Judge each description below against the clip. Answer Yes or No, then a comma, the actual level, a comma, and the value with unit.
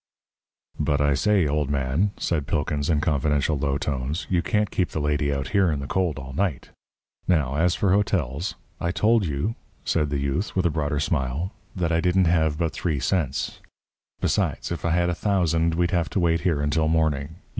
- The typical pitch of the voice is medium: No, very low, 80 Hz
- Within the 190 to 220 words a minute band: Yes, average, 200 wpm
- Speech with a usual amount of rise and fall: Yes, average, 3.5 semitones